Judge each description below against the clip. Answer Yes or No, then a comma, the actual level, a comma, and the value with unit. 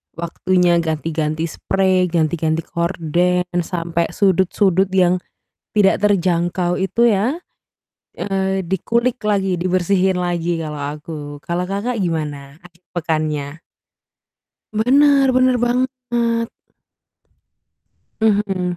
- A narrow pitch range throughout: No, average, 3.4 semitones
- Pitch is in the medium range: Yes, medium, 180 Hz